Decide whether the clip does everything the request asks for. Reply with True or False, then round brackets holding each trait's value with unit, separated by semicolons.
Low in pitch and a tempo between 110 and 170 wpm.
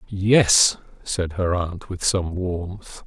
True (90 Hz; 135 wpm)